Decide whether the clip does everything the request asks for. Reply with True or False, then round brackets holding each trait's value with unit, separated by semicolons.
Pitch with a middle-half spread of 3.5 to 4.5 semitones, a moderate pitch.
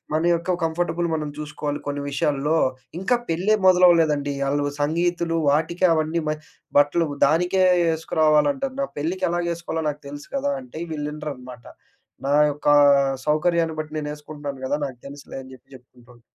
False (2.9 semitones; 155 Hz)